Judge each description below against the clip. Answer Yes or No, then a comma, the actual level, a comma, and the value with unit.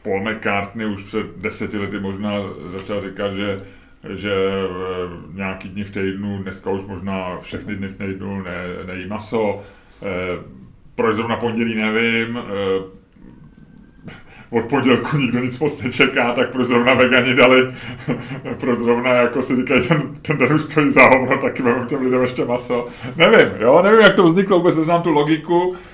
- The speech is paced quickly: No, average, 155 wpm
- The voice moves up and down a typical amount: Yes, average, 4.8 semitones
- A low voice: Yes, low, 115 Hz